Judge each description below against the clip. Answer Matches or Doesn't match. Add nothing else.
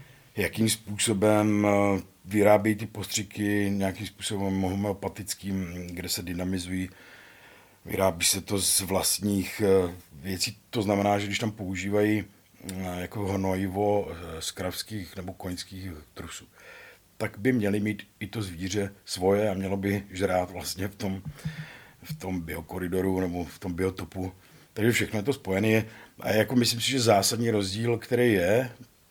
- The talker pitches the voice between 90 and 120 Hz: Matches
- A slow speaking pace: Doesn't match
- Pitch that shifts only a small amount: Matches